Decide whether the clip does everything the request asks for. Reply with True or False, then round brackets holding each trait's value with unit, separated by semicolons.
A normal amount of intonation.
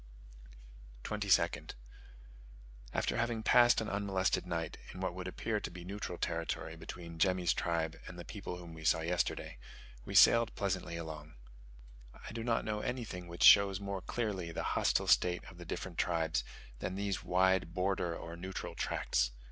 True (3.0 semitones)